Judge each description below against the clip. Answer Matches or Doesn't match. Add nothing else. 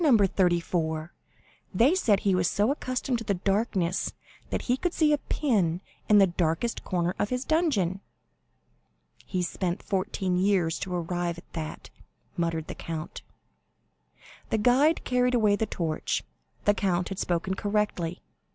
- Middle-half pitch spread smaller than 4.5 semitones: Doesn't match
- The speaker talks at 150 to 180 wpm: Doesn't match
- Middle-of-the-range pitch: Doesn't match